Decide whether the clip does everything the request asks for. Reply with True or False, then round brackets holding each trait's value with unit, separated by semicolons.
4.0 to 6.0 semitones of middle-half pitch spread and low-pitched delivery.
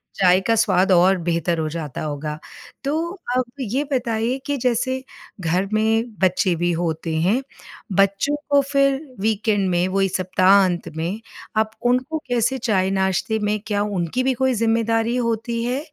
False (4.9 semitones; 210 Hz)